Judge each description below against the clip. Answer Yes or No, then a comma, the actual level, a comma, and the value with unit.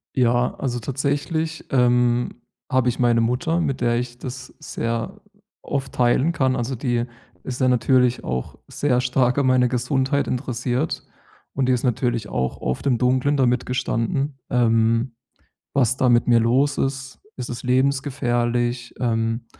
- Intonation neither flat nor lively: No, narrow, 1.8 semitones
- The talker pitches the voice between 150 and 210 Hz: No, low, 125 Hz